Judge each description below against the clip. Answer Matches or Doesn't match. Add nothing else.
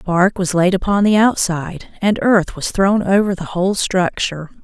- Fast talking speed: Doesn't match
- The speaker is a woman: Matches